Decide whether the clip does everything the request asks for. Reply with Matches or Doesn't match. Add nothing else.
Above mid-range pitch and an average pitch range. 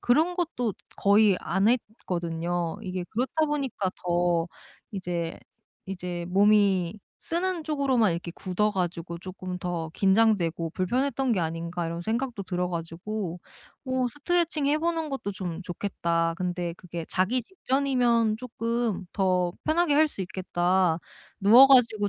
Doesn't match